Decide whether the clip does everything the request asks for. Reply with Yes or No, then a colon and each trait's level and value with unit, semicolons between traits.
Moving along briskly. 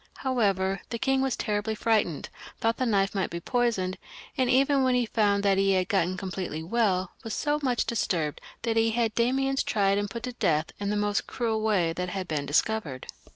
Yes: fast, 210 wpm